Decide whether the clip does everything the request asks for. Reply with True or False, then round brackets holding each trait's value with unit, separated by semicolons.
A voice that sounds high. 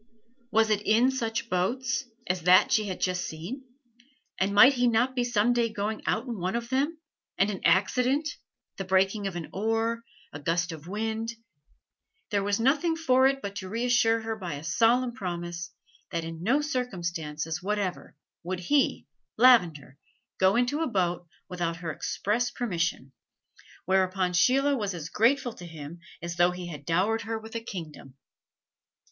True (205 Hz)